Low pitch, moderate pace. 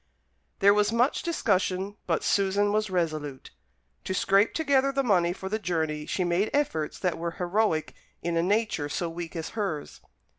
No: high, 190 Hz; average, 170 wpm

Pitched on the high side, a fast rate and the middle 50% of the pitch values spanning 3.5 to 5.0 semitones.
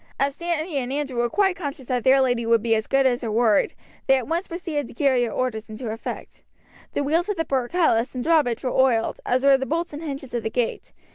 Yes: very high, 265 Hz; fast, 240 wpm; average, 4.1 semitones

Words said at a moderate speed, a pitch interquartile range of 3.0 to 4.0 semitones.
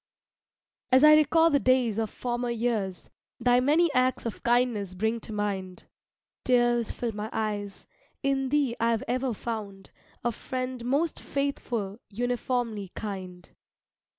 No: slow, 130 wpm; average, 3.5 semitones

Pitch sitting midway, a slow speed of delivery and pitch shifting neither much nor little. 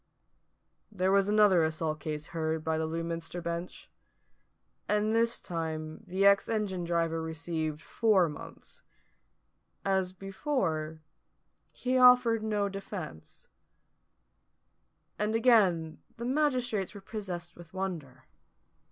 Yes: medium, 180 Hz; slow, 110 wpm; average, 4.6 semitones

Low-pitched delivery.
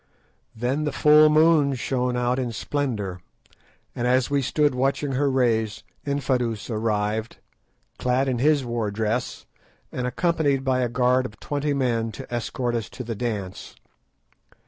Yes: low, 125 Hz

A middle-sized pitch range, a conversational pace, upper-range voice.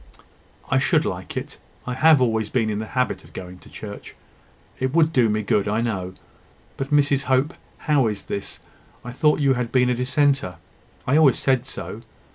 No: average, 4.2 semitones; average, 190 wpm; low, 125 Hz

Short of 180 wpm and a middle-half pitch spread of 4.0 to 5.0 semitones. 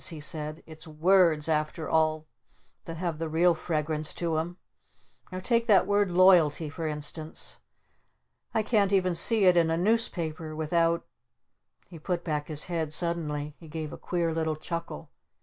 No: average, 165 wpm; narrow, 2.4 semitones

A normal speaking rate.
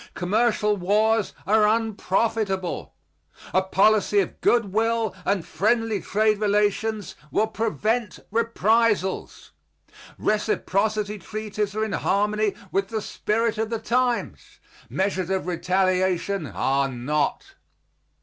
No: slow, 105 wpm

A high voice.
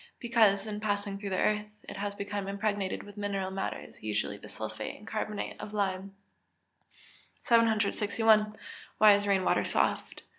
Yes: high, 205 Hz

